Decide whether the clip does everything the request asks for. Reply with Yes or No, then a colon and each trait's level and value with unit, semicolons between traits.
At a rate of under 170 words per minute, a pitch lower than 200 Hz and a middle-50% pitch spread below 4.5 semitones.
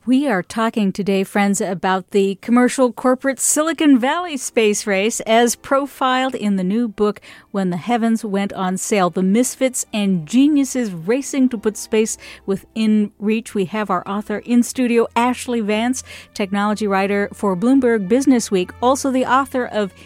No: average, 160 wpm; high, 225 Hz; average, 3.8 semitones